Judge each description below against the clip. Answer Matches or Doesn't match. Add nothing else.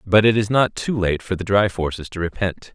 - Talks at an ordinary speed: Doesn't match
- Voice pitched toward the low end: Matches